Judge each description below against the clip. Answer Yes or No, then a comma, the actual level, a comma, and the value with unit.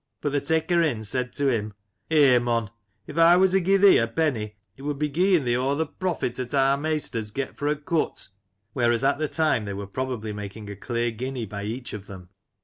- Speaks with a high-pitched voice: No, low, 130 Hz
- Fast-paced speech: Yes, fast, 230 wpm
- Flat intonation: No, average, 5.3 semitones